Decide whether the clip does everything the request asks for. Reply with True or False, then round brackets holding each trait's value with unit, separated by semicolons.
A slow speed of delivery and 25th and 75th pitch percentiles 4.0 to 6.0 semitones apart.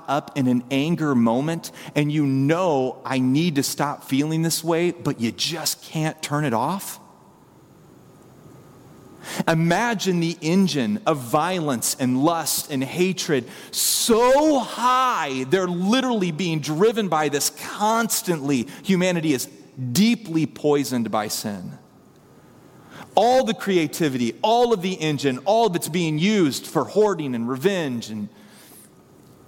True (130 wpm; 5.1 semitones)